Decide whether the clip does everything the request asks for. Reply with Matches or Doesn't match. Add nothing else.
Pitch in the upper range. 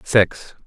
Doesn't match